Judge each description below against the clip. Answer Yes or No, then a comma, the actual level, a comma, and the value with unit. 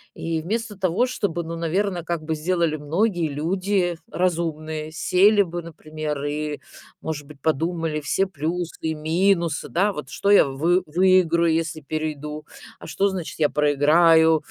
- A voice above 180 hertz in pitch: No, medium, 165 Hz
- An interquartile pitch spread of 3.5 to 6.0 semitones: No, average, 2.9 semitones